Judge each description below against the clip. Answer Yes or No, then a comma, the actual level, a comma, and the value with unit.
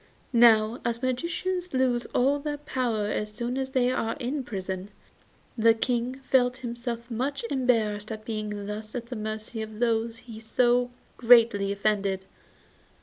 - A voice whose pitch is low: No, high, 235 Hz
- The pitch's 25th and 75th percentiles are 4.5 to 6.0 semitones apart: No, average, 2.8 semitones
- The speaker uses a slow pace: No, average, 150 wpm